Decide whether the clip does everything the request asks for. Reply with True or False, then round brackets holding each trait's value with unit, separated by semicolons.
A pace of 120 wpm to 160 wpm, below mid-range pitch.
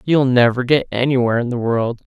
False (200 wpm; 125 Hz)